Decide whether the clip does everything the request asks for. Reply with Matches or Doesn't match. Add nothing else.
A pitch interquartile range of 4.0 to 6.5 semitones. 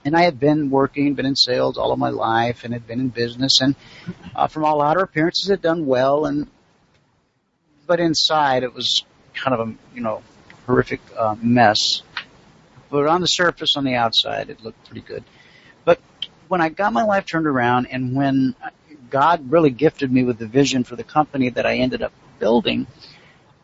Matches